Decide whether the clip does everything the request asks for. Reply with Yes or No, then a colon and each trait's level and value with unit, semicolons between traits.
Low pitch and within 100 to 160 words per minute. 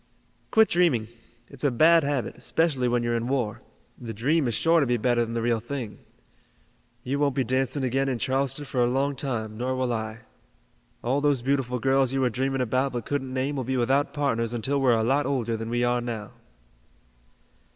No: low, 130 Hz; fast, 205 wpm